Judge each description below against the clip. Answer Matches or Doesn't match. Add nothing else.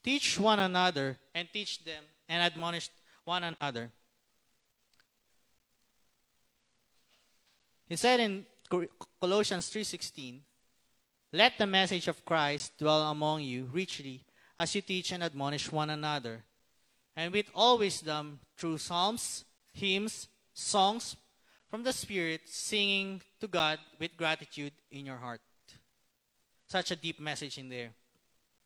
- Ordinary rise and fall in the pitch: Doesn't match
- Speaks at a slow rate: Matches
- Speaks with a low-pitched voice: Doesn't match